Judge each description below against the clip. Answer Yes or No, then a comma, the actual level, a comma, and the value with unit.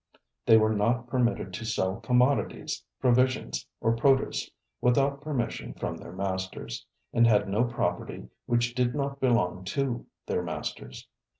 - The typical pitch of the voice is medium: No, low, 120 Hz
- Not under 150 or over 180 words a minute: No, slow, 135 wpm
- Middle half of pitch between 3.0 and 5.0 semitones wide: Yes, average, 3.6 semitones